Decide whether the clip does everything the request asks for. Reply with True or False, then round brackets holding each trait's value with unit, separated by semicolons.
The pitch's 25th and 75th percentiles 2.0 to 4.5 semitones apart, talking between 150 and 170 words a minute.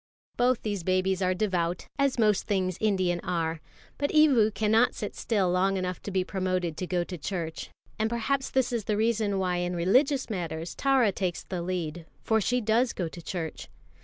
False (3.9 semitones; 190 wpm)